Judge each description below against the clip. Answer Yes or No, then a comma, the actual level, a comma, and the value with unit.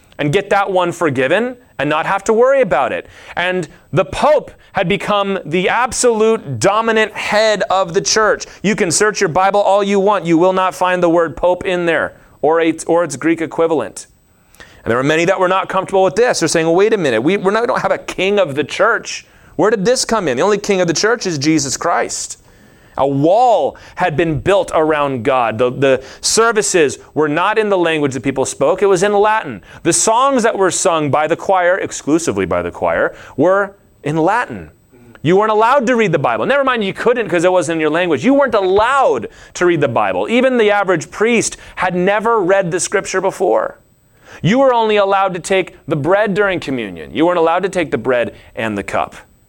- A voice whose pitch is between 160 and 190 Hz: Yes, medium, 185 Hz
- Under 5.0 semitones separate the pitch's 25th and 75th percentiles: Yes, average, 4.2 semitones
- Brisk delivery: Yes, fast, 215 wpm